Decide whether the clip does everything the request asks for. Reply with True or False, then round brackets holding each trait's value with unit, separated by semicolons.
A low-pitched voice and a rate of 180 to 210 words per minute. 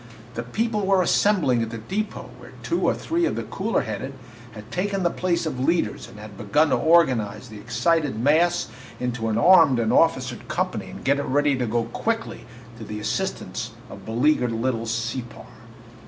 True (130 Hz; 185 wpm)